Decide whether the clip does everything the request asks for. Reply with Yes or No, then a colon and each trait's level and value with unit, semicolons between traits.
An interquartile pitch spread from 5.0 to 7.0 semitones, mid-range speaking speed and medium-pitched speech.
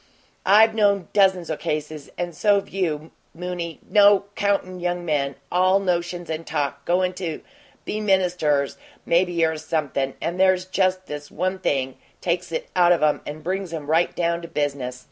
No: average, 3.3 semitones; average, 165 wpm; medium, 175 Hz